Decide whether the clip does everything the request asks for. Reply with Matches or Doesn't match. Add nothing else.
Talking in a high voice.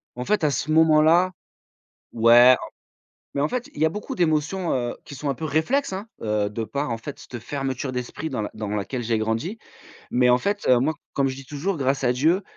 Doesn't match